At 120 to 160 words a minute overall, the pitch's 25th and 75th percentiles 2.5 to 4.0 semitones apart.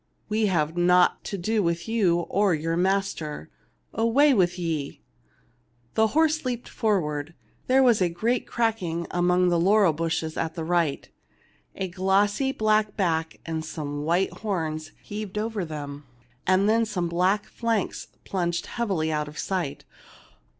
No: average, 150 wpm; average, 4.7 semitones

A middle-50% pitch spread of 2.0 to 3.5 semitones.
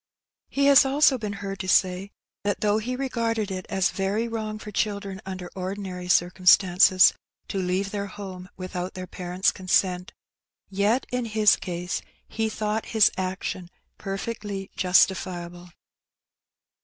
Yes: narrow, 2.6 semitones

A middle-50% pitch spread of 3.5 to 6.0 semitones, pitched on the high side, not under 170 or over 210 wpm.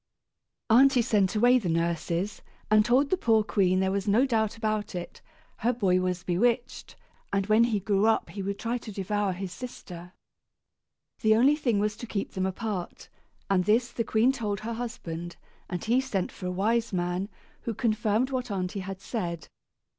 Yes: average, 3.8 semitones; high, 210 Hz; average, 180 wpm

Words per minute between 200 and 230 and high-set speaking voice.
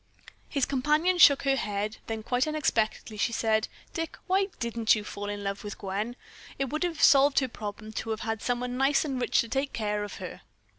Yes: fast, 205 wpm; high, 235 Hz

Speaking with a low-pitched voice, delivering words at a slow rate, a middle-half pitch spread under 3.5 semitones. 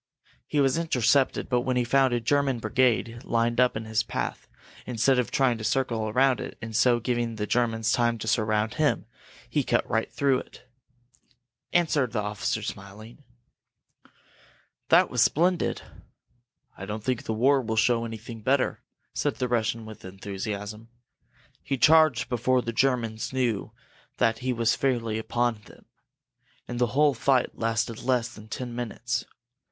No: low, 120 Hz; average, 155 wpm; narrow, 2.6 semitones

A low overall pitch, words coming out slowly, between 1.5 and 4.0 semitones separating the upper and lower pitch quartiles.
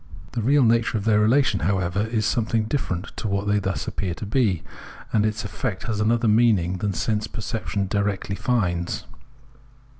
No: low, 105 Hz; average, 170 wpm; narrow, 2.5 semitones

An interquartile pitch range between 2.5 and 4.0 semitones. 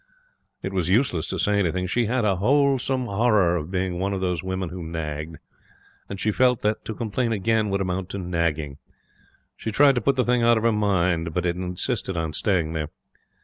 No: average, 4.4 semitones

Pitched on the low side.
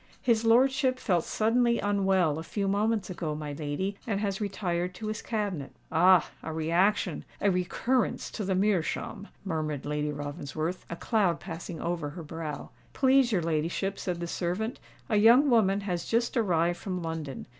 No: medium, 185 Hz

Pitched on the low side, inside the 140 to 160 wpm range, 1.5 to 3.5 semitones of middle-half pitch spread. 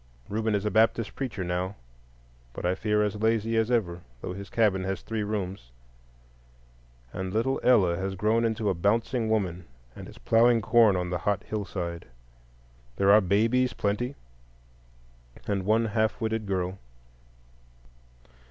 Yes: low, 105 Hz; average, 150 wpm; average, 3.1 semitones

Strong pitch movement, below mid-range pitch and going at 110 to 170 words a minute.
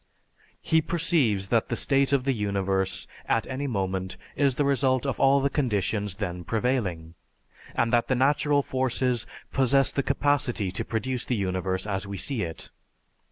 Yes: wide, 5.7 semitones; low, 120 Hz; average, 160 wpm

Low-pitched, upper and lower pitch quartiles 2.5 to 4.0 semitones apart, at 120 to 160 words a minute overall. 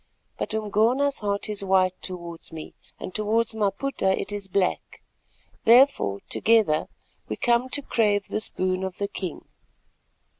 No: high, 205 Hz; average, 3.4 semitones; average, 140 wpm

